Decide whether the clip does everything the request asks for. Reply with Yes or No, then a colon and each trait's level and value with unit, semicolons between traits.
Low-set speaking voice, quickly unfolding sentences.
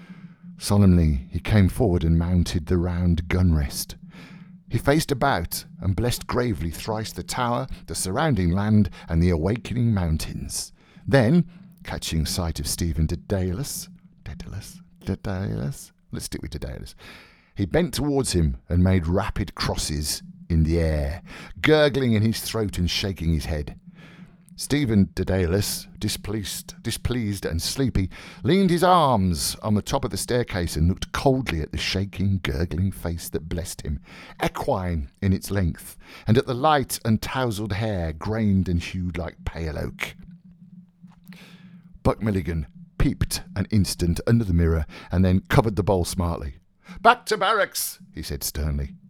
No: very low, 95 Hz; average, 145 wpm